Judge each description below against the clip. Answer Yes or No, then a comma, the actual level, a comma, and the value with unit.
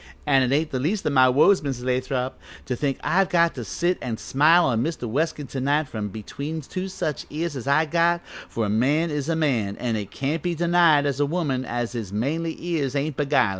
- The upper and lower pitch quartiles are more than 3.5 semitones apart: Yes, average, 4.4 semitones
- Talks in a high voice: No, medium, 145 Hz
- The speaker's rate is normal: No, fast, 230 wpm